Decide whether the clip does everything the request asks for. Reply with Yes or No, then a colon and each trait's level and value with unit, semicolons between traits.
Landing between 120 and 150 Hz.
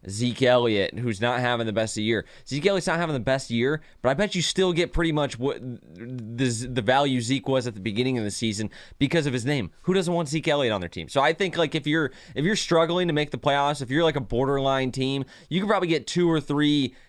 Yes: low, 135 Hz